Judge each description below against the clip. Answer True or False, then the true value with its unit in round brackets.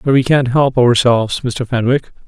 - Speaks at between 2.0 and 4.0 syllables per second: False (4.9 syllables/s)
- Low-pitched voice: True (125 Hz)